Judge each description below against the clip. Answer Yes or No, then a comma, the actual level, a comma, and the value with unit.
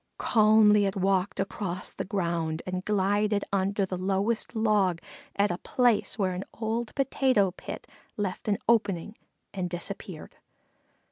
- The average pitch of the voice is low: No, high, 200 Hz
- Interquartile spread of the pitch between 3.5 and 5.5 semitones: No, narrow, 2.4 semitones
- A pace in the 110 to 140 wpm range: Yes, slow, 135 wpm